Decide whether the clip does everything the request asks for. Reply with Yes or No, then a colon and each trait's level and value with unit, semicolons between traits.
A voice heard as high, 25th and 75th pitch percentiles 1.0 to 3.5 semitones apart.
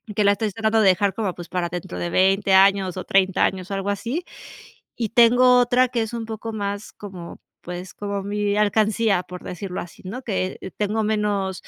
Yes: high, 200 Hz; average, 2.7 semitones